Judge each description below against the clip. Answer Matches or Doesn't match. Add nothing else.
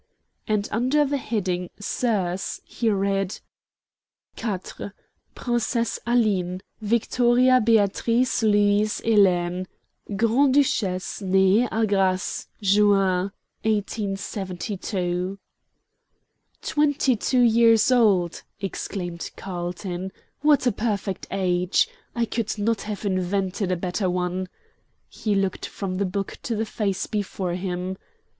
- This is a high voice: Matches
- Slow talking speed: Matches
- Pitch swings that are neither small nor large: Matches